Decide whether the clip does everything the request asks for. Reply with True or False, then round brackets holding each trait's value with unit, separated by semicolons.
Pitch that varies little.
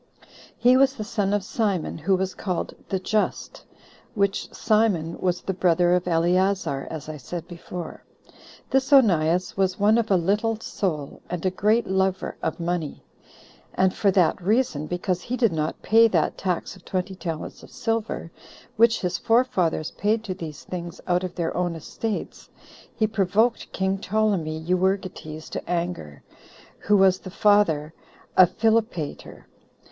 False (3.6 semitones)